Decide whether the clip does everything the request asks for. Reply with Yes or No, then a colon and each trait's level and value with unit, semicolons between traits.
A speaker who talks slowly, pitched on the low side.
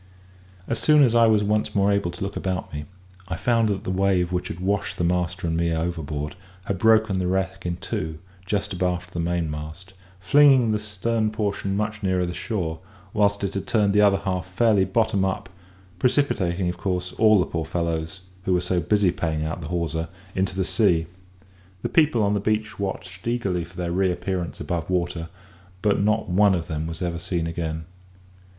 No: average, 195 wpm; very low, 95 Hz